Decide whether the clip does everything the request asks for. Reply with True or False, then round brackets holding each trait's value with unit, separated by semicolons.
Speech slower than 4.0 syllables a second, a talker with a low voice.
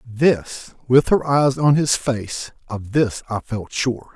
True (3.3 syllables/s; 125 Hz)